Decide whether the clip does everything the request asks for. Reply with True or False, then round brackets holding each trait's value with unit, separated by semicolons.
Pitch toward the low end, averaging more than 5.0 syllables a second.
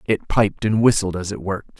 True (100 Hz; 5.6 syllables/s)